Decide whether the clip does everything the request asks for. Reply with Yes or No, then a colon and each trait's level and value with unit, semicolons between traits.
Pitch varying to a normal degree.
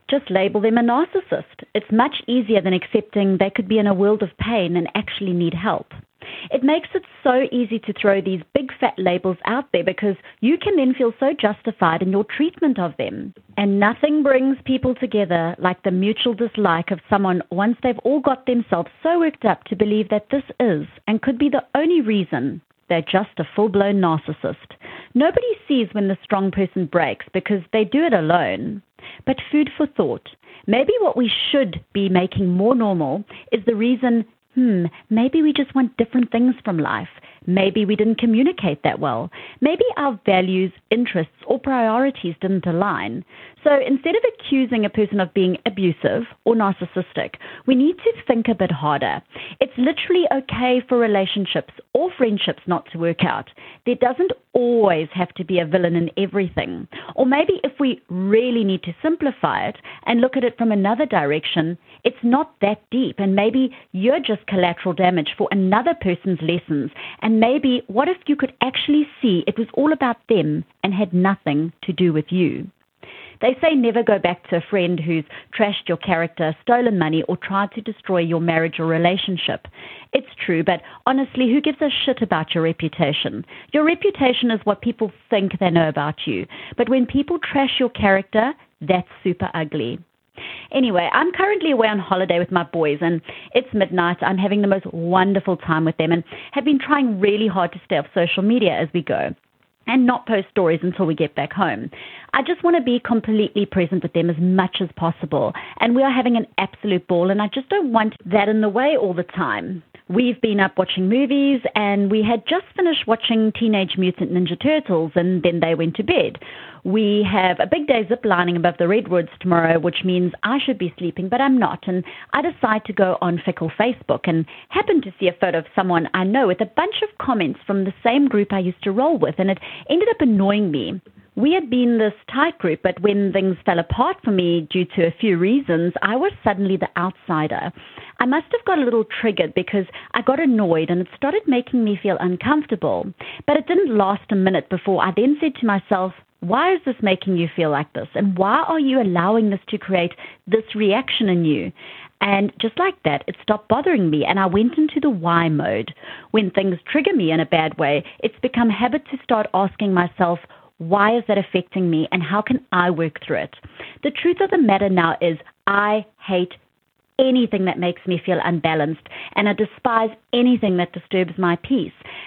No: wide, 5.8 semitones